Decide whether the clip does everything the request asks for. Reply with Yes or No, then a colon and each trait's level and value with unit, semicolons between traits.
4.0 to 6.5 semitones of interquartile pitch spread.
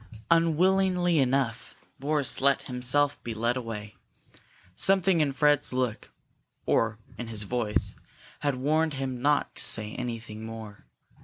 Yes: average, 4.5 semitones